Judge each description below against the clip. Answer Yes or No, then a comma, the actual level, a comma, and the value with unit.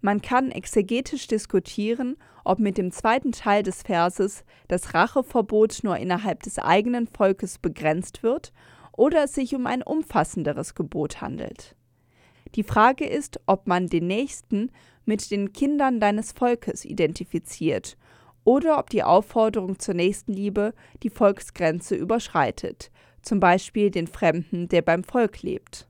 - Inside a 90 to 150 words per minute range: Yes, average, 135 wpm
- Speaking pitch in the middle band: No, high, 205 Hz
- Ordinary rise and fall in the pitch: Yes, average, 4.8 semitones